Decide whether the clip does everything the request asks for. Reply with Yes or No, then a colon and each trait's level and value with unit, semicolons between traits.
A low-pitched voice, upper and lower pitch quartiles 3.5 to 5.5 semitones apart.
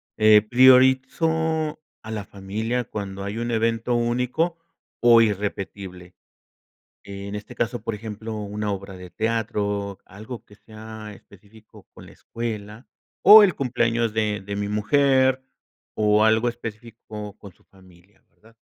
No: low, 110 Hz; average, 2.7 semitones